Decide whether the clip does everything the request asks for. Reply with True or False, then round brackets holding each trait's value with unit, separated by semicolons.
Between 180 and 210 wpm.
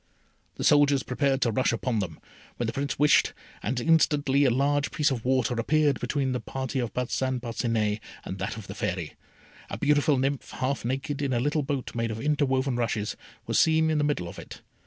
True (200 wpm)